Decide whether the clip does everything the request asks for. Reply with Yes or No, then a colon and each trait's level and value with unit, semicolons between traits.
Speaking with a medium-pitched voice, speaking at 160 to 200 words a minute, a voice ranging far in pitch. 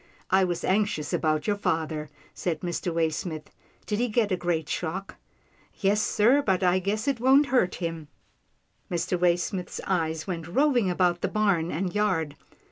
No: medium, 180 Hz; average, 170 wpm; average, 4.0 semitones